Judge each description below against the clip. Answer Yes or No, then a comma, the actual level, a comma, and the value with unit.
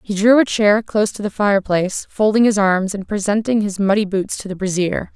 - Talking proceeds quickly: Yes, fast, 220 wpm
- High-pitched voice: Yes, high, 200 Hz